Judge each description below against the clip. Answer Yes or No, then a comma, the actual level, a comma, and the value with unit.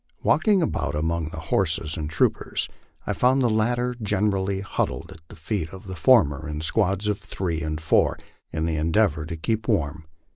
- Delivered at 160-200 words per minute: Yes, average, 180 wpm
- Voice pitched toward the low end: Yes, very low, 90 Hz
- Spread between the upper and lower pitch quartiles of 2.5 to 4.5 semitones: No, average, 5.1 semitones